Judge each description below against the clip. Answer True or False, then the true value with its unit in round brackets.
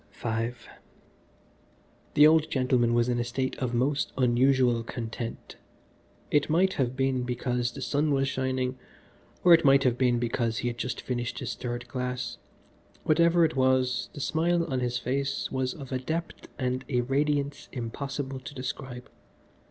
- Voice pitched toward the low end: True (130 Hz)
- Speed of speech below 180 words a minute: True (160 wpm)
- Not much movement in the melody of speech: True (2.3 semitones)